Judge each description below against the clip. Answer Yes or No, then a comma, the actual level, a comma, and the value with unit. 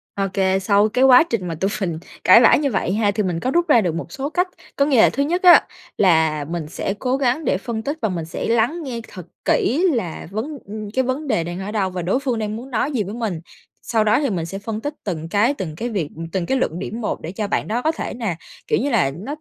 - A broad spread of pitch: Yes, wide, 5.8 semitones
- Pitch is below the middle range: No, high, 215 Hz